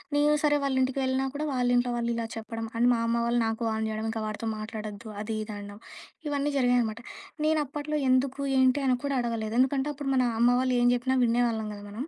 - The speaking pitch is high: Yes, high, 245 Hz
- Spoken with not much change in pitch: No, average, 3.1 semitones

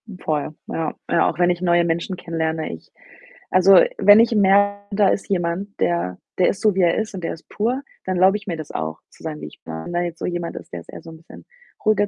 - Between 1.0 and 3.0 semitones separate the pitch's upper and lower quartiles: No, average, 3.7 semitones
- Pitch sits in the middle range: Yes, medium, 175 Hz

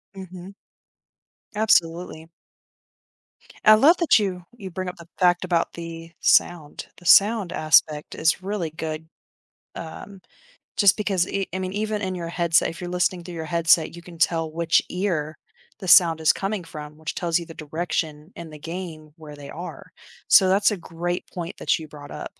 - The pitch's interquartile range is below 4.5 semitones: Yes, narrow, 2.6 semitones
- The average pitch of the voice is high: No, medium, 170 Hz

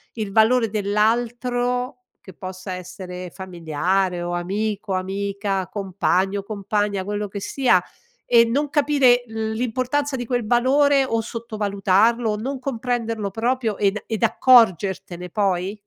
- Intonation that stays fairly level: No, average, 4.0 semitones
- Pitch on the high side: Yes, high, 215 Hz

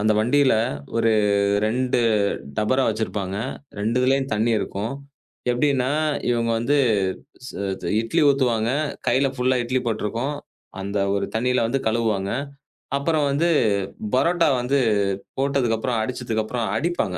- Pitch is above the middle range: No, low, 120 Hz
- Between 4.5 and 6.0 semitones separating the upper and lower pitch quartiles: No, average, 3.5 semitones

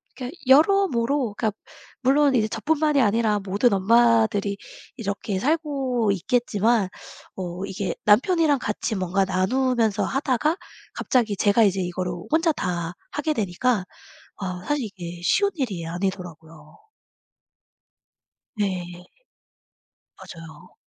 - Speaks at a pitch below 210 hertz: No, high, 215 Hz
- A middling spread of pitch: No, wide, 5.8 semitones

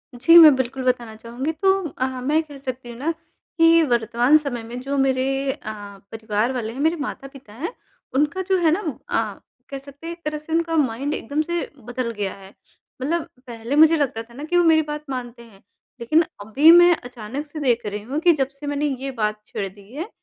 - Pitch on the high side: Yes, very high, 270 Hz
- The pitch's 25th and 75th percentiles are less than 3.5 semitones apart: No, average, 4.6 semitones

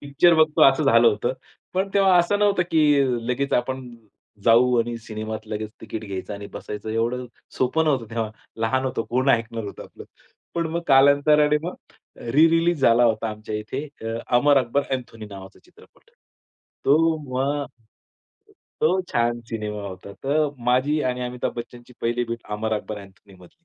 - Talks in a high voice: No, low, 125 Hz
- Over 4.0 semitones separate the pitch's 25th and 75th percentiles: Yes, average, 4.6 semitones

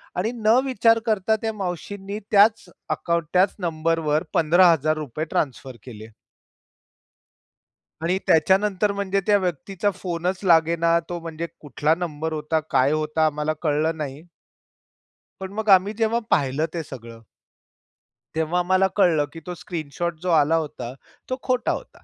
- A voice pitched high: No, medium, 170 Hz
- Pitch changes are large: No, average, 3.8 semitones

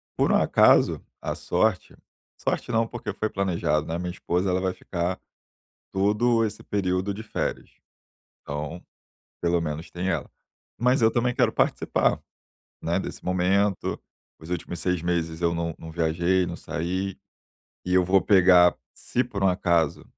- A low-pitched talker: Yes, very low, 90 Hz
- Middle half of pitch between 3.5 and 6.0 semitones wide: No, narrow, 2.6 semitones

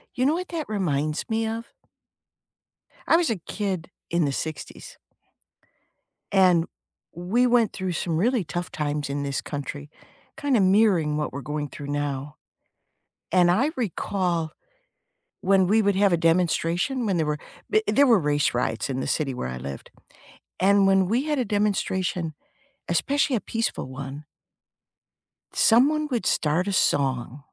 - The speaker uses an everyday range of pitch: No, wide, 6.9 semitones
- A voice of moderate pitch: Yes, medium, 180 Hz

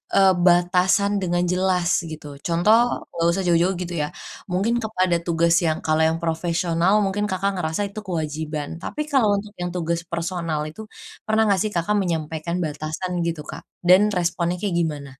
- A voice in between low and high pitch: Yes, medium, 175 Hz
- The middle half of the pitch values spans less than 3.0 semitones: Yes, narrow, 2.5 semitones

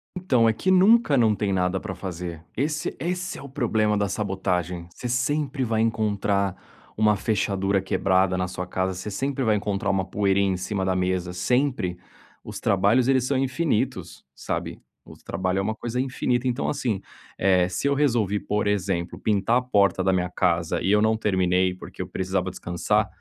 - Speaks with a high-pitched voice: No, low, 100 Hz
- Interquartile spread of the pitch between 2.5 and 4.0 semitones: No, average, 4.8 semitones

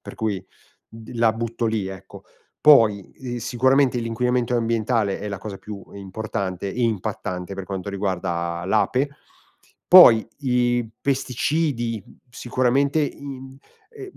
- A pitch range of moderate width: Yes, average, 4.2 semitones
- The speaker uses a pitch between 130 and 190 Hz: No, low, 115 Hz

